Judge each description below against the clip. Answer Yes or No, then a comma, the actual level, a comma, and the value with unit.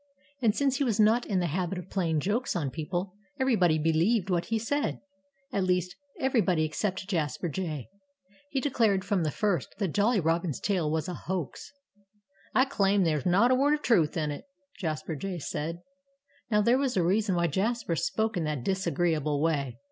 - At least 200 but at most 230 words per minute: No, average, 185 wpm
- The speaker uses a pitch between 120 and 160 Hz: No, medium, 185 Hz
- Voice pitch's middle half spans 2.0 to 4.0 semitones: No, average, 5.1 semitones